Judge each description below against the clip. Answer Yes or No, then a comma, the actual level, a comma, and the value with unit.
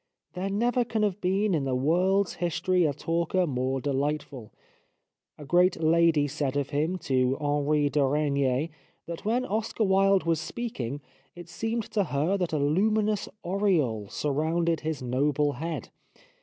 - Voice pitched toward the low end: No, medium, 160 Hz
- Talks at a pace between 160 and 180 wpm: No, average, 150 wpm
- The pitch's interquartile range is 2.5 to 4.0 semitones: No, average, 5.0 semitones